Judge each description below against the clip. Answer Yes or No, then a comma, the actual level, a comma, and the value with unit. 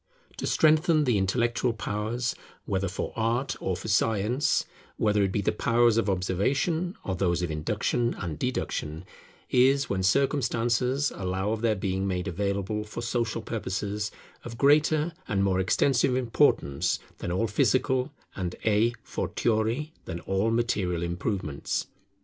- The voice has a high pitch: No, low, 110 Hz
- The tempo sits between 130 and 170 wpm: Yes, average, 140 wpm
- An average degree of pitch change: Yes, average, 4.4 semitones